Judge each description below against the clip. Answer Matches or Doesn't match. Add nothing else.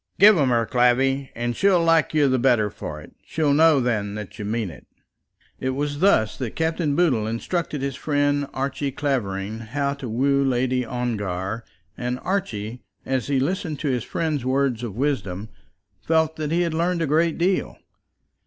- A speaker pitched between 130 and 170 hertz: Matches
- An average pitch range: Matches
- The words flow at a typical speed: Matches